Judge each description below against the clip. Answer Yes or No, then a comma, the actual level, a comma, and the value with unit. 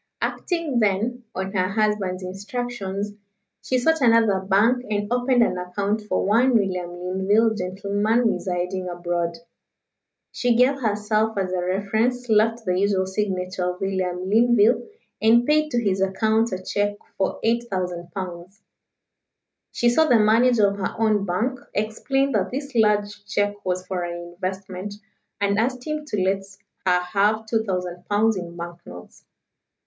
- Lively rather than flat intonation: No, average, 3.6 semitones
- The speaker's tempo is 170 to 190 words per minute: No, average, 145 wpm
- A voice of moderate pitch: No, high, 205 Hz